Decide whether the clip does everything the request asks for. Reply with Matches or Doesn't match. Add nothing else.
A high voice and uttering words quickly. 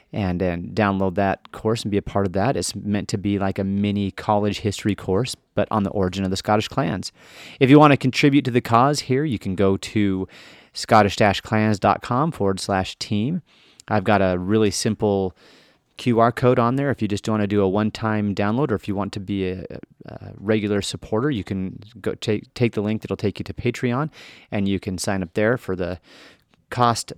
Doesn't match